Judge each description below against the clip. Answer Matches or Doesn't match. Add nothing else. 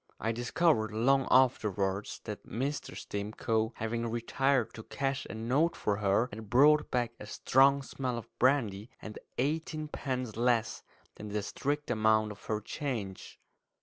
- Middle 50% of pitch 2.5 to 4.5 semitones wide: Matches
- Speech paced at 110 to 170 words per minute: Matches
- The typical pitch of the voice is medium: Doesn't match